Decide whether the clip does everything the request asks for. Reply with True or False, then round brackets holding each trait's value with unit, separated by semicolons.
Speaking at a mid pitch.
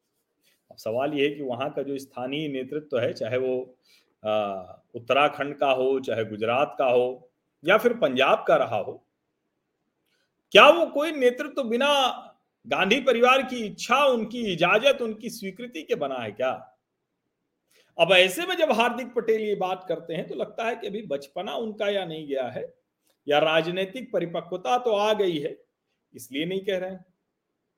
False (195 Hz)